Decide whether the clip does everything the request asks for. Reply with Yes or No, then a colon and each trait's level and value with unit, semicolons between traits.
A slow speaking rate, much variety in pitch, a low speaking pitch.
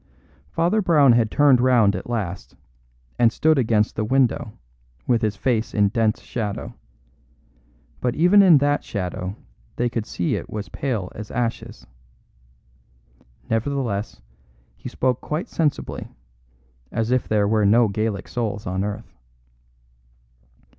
No: slow, 130 wpm; average, 3.8 semitones; low, 115 Hz